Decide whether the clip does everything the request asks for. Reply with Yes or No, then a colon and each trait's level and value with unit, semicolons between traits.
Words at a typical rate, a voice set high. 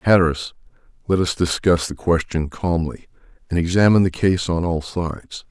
No: average, 155 wpm; very low, 85 Hz